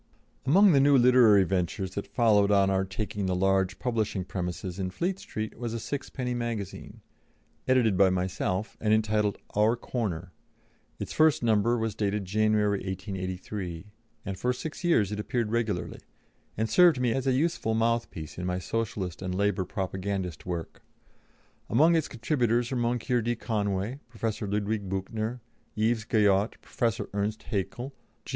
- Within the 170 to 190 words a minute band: No, average, 150 wpm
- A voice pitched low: Yes, low, 105 Hz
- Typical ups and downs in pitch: Yes, average, 3.7 semitones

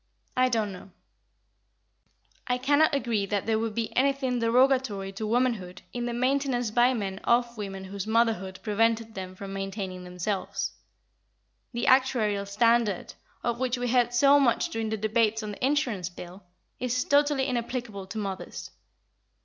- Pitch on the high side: Yes, high, 230 Hz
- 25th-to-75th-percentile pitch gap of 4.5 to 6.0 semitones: No, average, 3.9 semitones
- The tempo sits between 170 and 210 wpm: No, average, 150 wpm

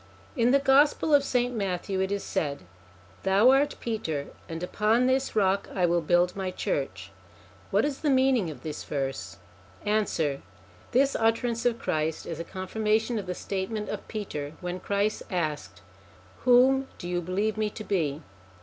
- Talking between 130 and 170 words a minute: Yes, average, 165 wpm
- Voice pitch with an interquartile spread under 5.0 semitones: No, wide, 5.6 semitones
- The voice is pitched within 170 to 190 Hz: No, high, 200 Hz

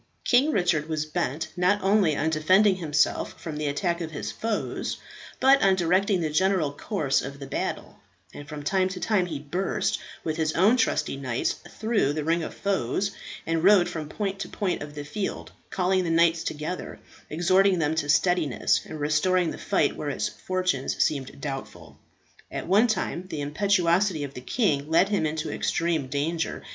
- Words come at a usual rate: Yes, average, 180 wpm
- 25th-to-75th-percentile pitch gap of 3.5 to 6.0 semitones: Yes, average, 4.1 semitones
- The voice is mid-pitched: Yes, medium, 165 Hz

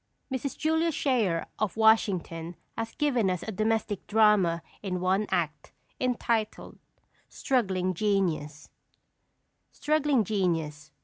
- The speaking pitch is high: Yes, high, 205 Hz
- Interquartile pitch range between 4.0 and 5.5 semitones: Yes, average, 4.6 semitones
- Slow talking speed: Yes, slow, 105 wpm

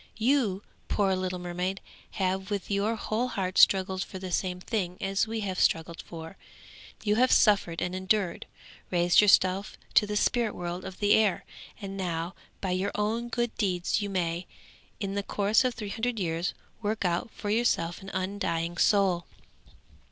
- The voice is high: Yes, high, 195 Hz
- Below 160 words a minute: No, average, 165 wpm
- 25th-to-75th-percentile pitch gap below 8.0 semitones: Yes, narrow, 2.5 semitones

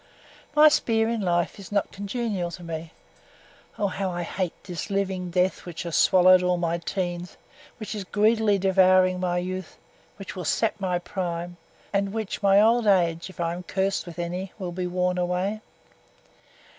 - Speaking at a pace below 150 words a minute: No, average, 180 wpm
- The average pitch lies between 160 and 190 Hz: Yes, medium, 185 Hz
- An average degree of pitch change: No, narrow, 2.1 semitones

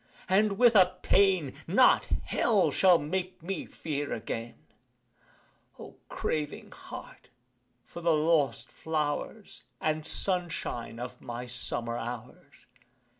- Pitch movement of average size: No, wide, 6.5 semitones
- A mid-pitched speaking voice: Yes, medium, 155 Hz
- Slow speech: Yes, slow, 110 wpm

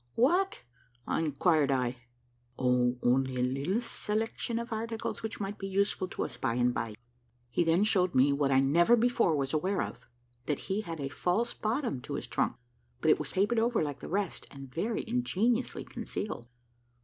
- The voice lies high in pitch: No, medium, 180 Hz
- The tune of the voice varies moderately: No, wide, 8.5 semitones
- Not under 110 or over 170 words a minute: No, average, 180 wpm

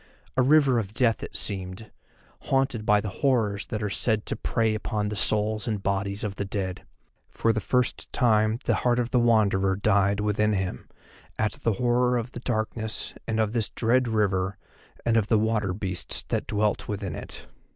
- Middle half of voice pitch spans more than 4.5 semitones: No, narrow, 2.5 semitones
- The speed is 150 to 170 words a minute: No, average, 185 wpm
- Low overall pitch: Yes, low, 110 Hz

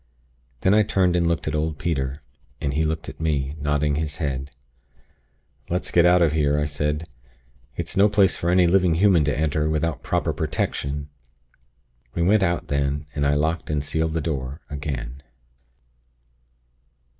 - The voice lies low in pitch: Yes, very low, 75 Hz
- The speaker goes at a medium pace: Yes, average, 165 wpm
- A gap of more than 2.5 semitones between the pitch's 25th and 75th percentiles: Yes, average, 2.9 semitones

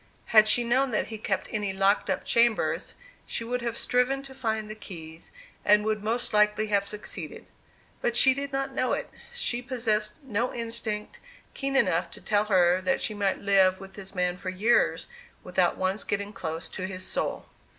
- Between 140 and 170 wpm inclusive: No, average, 185 wpm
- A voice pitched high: Yes, high, 215 Hz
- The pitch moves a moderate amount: Yes, average, 3.6 semitones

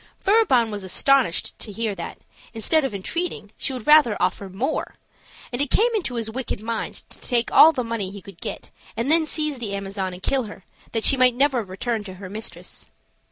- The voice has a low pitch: No, high, 230 Hz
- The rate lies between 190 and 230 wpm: Yes, fast, 205 wpm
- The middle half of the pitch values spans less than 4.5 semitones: No, wide, 5.4 semitones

